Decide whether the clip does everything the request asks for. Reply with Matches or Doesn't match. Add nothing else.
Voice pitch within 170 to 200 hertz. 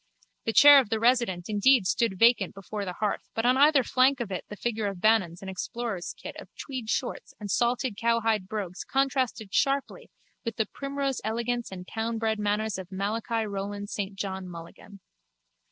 Doesn't match